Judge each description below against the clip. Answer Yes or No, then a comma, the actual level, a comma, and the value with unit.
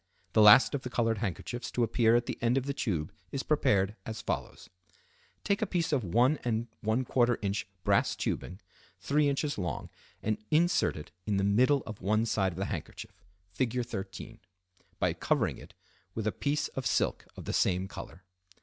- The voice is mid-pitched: No, low, 115 Hz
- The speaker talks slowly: No, average, 175 wpm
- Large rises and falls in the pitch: No, average, 4.6 semitones